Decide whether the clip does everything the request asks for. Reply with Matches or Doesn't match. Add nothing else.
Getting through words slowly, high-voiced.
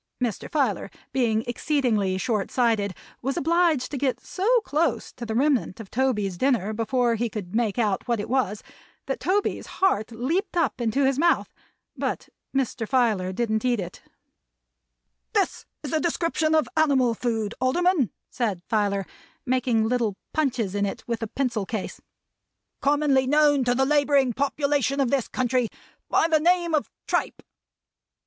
Doesn't match